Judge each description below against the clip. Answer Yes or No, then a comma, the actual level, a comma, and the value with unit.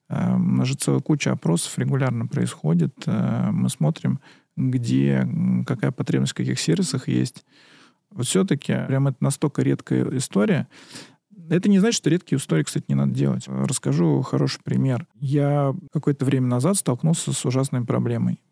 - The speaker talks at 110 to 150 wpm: Yes, average, 145 wpm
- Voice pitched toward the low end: Yes, low, 125 Hz